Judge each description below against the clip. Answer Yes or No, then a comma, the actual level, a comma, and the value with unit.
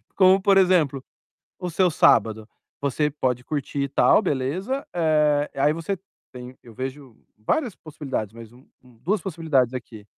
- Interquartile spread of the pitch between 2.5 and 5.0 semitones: No, wide, 5.6 semitones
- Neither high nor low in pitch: Yes, medium, 145 Hz